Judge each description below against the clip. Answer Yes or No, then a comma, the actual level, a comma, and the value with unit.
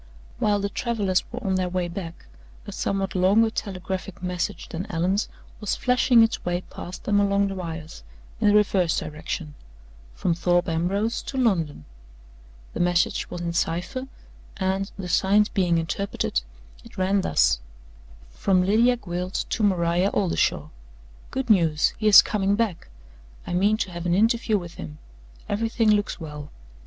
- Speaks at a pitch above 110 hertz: Yes, high, 190 Hz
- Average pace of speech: Yes, average, 155 wpm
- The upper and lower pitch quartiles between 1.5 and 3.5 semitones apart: Yes, average, 3.2 semitones